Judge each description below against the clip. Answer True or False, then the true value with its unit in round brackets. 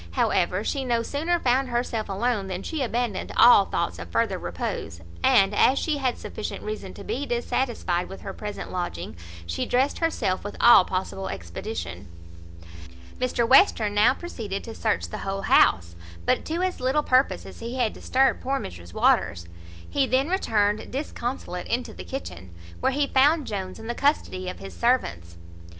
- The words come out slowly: False (170 wpm)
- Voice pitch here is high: True (225 Hz)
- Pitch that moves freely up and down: True (5.8 semitones)